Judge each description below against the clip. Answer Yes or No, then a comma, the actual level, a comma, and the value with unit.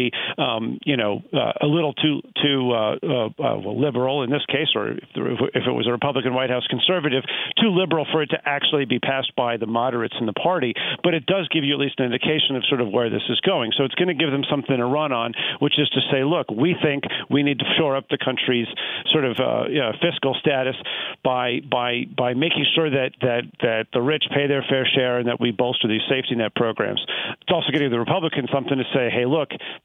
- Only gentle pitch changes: No, average, 3.2 semitones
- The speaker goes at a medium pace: No, fast, 240 wpm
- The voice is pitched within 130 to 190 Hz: Yes, low, 135 Hz